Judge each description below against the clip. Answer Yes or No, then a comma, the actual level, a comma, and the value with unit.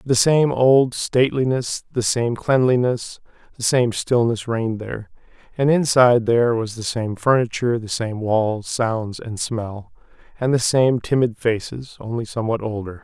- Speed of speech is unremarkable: Yes, average, 150 wpm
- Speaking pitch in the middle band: No, low, 115 Hz